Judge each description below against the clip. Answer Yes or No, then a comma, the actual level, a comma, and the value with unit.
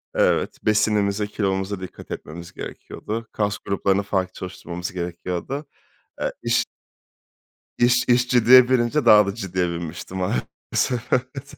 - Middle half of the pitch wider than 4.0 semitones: Yes, average, 4.7 semitones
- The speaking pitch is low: Yes, low, 100 Hz